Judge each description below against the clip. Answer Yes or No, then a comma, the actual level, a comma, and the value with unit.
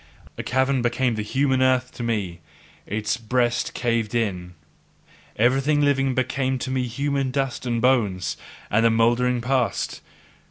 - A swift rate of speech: No, slow, 135 wpm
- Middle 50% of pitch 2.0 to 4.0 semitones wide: Yes, narrow, 2.5 semitones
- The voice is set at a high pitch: No, low, 125 Hz